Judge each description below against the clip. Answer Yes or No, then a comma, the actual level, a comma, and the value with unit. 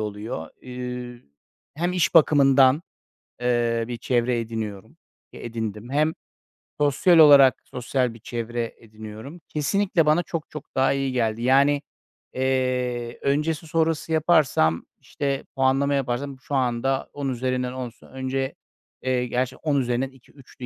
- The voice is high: No, low, 130 Hz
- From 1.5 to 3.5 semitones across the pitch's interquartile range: Yes, average, 3.0 semitones